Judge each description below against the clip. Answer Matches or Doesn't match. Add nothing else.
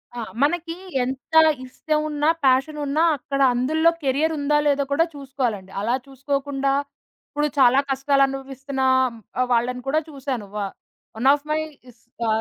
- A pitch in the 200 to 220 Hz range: Doesn't match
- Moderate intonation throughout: Doesn't match